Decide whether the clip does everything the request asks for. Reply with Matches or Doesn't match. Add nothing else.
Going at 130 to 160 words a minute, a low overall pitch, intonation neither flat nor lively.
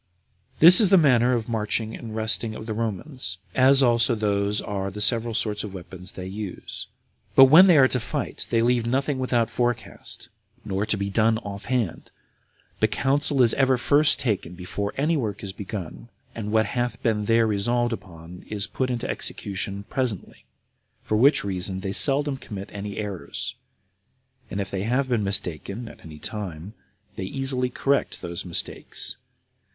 Doesn't match